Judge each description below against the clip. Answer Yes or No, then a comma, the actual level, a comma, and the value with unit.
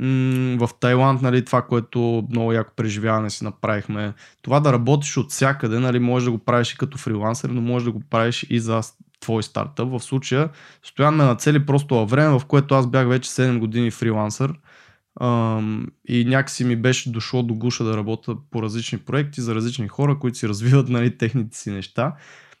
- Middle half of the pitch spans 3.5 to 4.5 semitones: No, average, 2.7 semitones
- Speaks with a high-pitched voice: No, low, 120 Hz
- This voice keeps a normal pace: No, fast, 185 wpm